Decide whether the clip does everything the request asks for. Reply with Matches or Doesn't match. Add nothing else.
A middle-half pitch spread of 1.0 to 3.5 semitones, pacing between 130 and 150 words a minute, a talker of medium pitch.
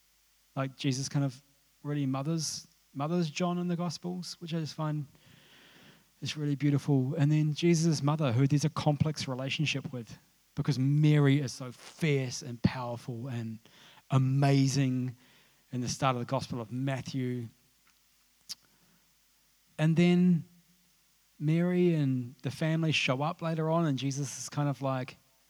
Matches